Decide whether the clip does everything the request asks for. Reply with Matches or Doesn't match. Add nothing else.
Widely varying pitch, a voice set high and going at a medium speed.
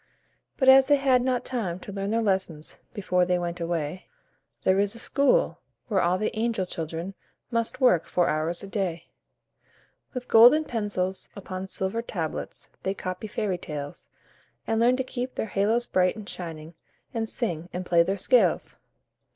Doesn't match